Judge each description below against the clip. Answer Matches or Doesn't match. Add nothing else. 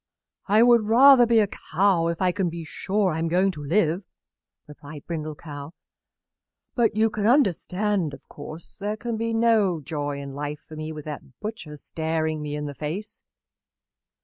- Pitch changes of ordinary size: Doesn't match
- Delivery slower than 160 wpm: Doesn't match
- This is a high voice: Doesn't match